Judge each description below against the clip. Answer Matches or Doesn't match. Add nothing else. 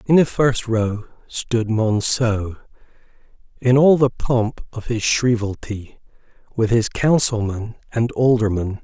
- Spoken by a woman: Doesn't match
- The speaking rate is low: Matches